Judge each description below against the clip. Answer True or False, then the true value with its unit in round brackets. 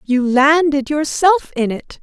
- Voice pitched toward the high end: True (290 Hz)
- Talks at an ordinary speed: True (150 wpm)